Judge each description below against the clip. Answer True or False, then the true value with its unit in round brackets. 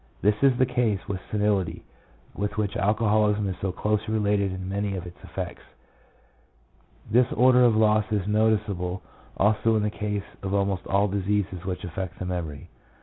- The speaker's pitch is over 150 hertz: False (105 Hz)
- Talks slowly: False (165 wpm)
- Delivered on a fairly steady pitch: True (2.1 semitones)